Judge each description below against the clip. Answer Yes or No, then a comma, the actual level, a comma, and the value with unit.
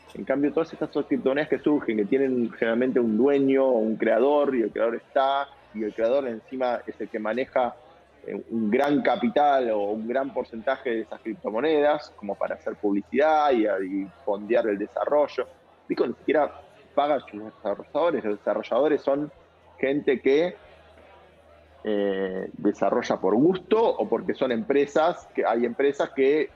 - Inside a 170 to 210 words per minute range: No, average, 155 wpm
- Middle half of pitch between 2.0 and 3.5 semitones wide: No, average, 4.6 semitones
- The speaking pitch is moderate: No, low, 130 Hz